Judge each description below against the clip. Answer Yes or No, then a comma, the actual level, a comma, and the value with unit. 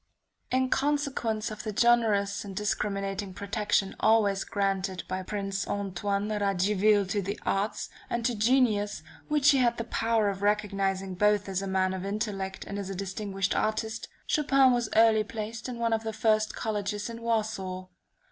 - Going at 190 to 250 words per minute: No, average, 165 wpm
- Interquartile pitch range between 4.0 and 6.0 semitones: No, narrow, 2.4 semitones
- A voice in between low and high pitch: No, high, 210 Hz